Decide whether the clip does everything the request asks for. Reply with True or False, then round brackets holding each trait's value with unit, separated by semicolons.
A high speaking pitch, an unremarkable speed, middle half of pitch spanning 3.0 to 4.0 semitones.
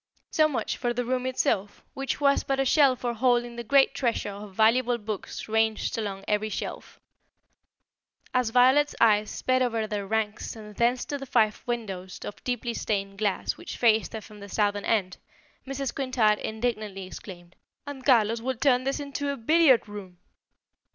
True (230 Hz; 170 wpm; 3.6 semitones)